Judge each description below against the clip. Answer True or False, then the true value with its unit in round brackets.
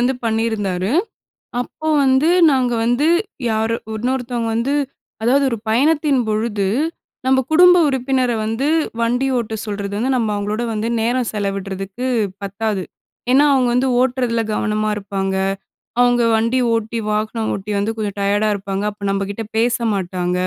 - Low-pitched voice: False (225 Hz)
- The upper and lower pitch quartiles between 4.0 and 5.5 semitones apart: False (3.5 semitones)